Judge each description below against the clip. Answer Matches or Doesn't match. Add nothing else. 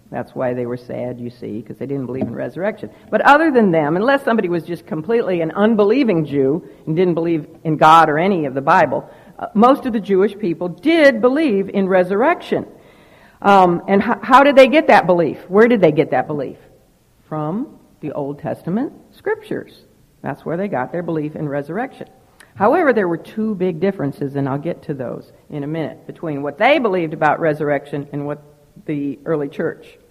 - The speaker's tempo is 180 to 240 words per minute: Matches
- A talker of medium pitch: Matches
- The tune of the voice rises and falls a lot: Matches